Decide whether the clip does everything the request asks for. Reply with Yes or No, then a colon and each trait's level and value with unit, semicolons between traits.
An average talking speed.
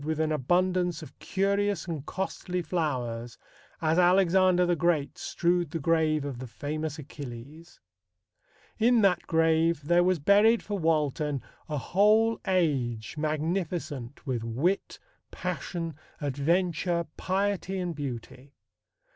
No: slow, 120 wpm